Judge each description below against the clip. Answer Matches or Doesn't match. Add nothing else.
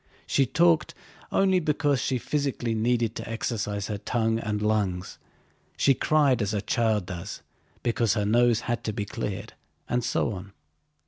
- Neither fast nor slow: Matches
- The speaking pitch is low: Matches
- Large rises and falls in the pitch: Doesn't match